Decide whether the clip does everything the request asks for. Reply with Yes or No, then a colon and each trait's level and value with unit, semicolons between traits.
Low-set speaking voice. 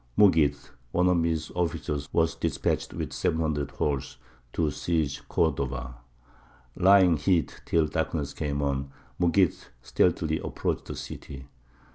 Yes: very low, 75 Hz